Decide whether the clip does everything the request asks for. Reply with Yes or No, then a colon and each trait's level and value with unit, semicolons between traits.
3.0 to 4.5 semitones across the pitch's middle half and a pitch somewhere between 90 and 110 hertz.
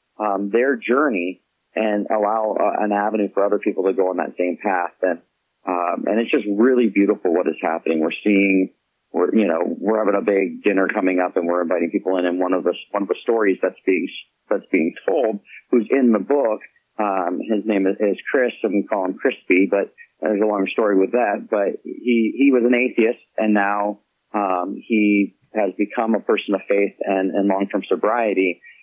No: narrow, 2.4 semitones; low, 100 Hz